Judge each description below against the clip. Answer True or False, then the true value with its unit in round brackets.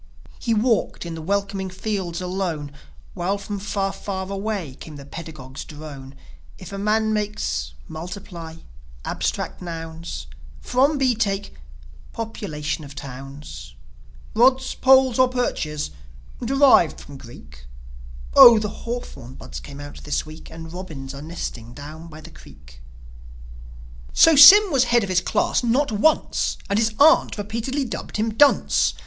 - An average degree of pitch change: False (7.1 semitones)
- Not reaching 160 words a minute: True (140 wpm)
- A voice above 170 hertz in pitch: True (185 Hz)